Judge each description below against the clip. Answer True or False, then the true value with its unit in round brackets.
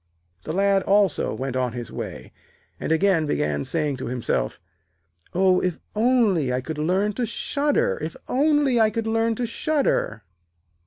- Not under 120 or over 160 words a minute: True (155 wpm)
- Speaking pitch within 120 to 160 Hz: False (195 Hz)